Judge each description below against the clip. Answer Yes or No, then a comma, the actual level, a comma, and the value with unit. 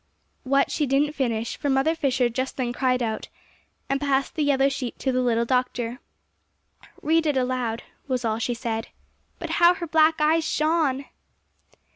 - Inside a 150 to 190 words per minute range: Yes, average, 165 wpm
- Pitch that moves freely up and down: No, average, 3.2 semitones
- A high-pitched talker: Yes, very high, 265 Hz